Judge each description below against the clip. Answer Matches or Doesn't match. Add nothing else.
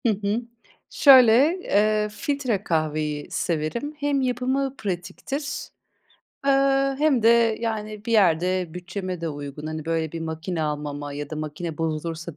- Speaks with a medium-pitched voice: Matches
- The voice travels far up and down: Matches